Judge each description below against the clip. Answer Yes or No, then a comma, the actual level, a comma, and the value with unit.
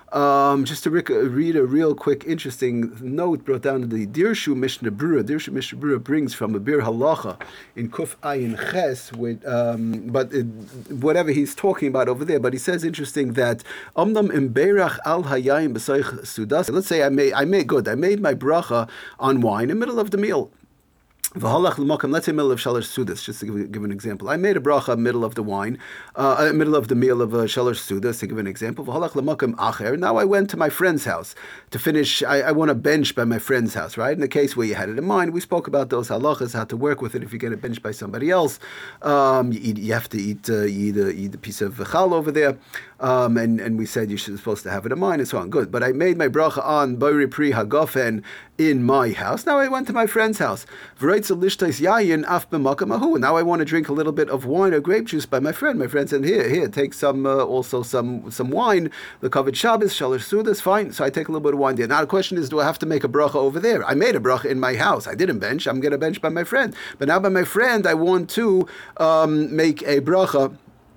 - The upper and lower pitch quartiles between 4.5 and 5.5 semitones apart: Yes, average, 5.1 semitones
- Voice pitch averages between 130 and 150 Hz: Yes, medium, 140 Hz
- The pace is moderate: No, fast, 240 wpm